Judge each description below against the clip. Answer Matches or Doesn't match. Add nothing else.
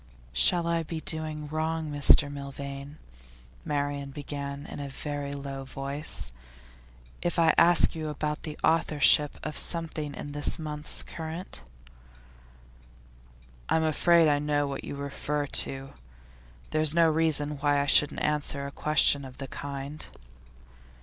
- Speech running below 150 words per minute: Matches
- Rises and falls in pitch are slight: Matches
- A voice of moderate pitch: Matches